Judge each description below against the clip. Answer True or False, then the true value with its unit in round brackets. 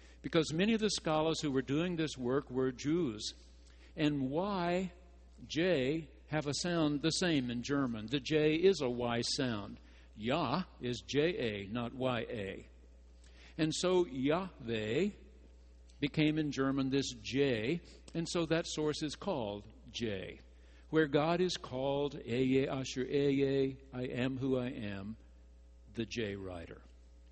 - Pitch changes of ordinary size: False (6.9 semitones)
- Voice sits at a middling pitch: False (130 Hz)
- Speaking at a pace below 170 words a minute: True (140 wpm)